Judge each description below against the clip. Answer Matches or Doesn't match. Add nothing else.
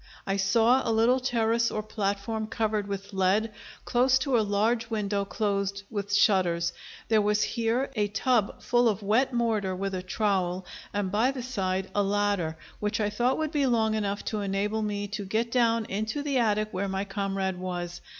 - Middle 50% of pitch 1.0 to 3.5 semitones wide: Matches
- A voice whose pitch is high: Matches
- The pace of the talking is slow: Doesn't match